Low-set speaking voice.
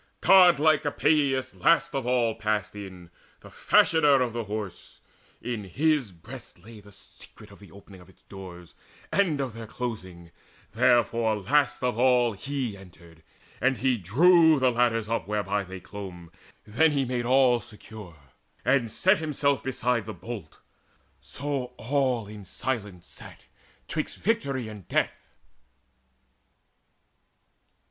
Yes: low, 115 Hz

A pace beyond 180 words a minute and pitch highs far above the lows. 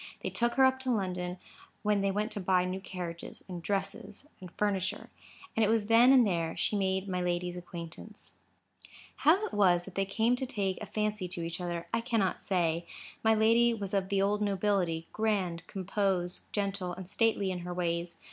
No: average, 190 wpm; average, 3.1 semitones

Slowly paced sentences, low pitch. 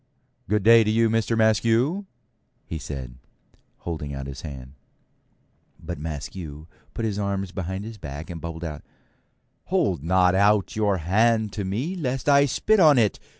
No: average, 155 wpm; low, 100 Hz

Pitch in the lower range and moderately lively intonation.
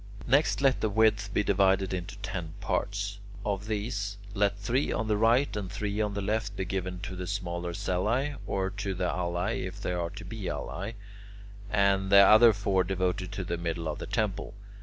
No: low, 100 Hz; narrow, 2.3 semitones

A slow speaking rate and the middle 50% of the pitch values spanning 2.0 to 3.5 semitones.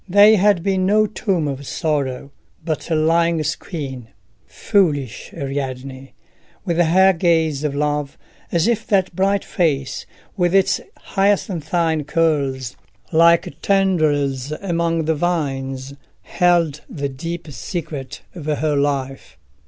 No: slow, 120 wpm; average, 4.0 semitones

